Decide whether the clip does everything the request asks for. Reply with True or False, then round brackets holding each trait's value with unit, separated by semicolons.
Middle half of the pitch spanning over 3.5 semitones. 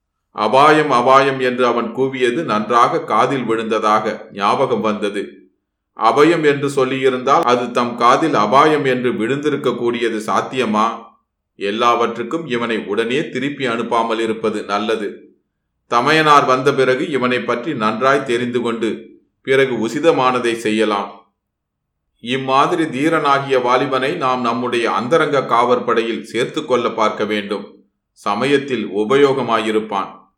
False (3.2 semitones)